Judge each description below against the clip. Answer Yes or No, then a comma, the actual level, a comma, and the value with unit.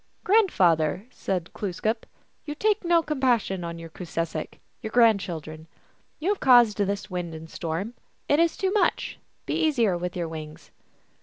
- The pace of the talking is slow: No, average, 165 wpm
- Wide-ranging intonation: Yes, wide, 8.4 semitones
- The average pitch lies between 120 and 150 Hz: No, high, 200 Hz